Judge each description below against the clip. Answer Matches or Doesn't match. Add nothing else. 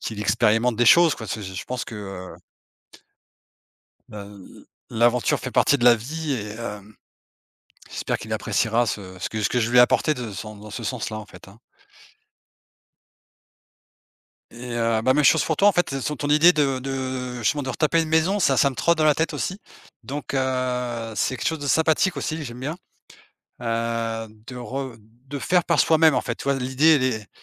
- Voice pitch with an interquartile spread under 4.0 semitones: Doesn't match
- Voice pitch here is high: Doesn't match